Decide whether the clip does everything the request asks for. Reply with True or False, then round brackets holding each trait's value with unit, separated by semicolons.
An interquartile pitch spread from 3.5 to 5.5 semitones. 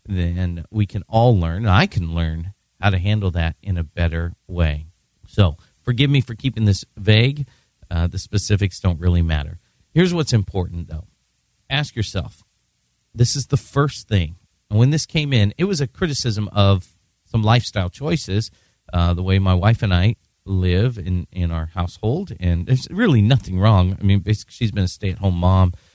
True (4.4 semitones)